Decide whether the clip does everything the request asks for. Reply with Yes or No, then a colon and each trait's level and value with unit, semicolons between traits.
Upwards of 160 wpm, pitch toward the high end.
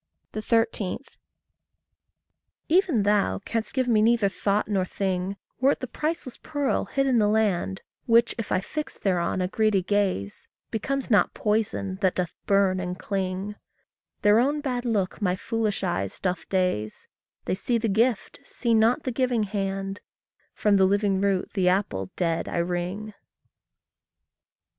No: average, 150 wpm; high, 205 Hz